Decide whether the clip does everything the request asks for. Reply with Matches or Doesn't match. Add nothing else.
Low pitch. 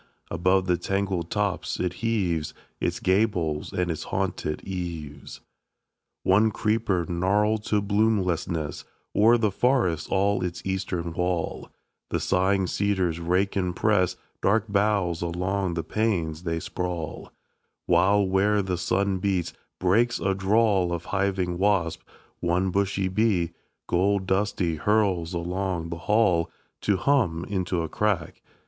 Matches